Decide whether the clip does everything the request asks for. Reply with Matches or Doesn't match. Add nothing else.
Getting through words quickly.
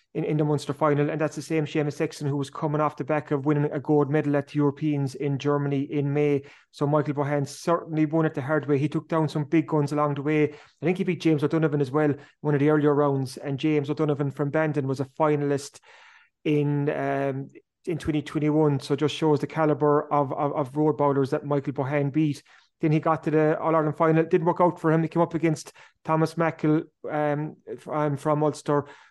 Matches